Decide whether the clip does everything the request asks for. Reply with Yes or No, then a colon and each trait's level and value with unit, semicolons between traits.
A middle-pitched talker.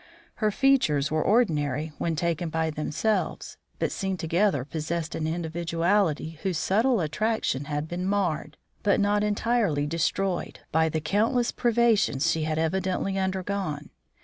Yes: medium, 170 Hz